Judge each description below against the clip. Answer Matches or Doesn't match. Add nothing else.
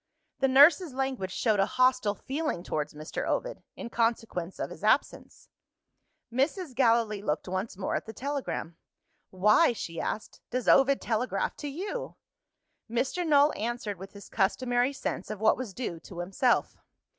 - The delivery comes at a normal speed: Matches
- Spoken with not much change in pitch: Doesn't match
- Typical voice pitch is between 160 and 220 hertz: Doesn't match